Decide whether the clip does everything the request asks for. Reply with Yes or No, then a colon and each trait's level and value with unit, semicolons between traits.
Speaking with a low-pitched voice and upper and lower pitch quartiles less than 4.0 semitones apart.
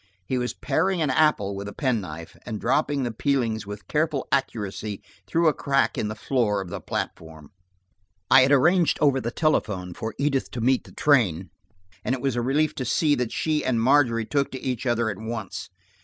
No: low, 125 Hz; average, 4.8 semitones